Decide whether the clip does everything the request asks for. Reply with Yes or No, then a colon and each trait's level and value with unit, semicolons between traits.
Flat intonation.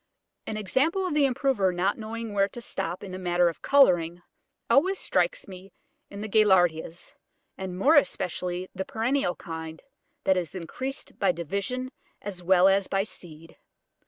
No: average, 5.1 semitones